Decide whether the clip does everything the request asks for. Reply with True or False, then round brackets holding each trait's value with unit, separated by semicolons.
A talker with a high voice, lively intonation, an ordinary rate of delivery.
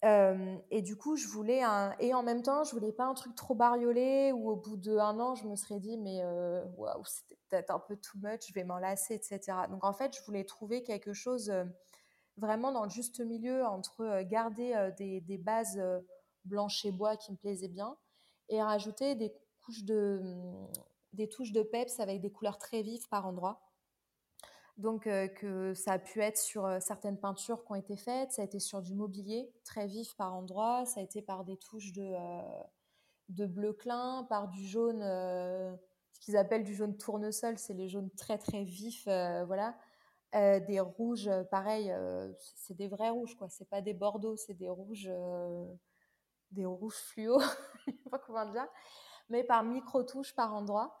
False (210 Hz; 3.0 semitones; 200 wpm)